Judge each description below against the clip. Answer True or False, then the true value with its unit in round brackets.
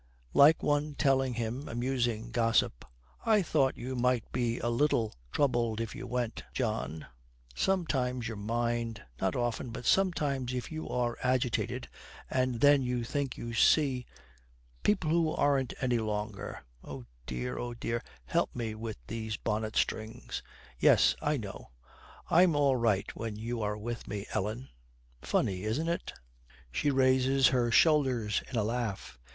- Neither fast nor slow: True (150 wpm)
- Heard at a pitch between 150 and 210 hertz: False (120 Hz)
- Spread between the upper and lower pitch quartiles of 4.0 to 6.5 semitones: False (3.3 semitones)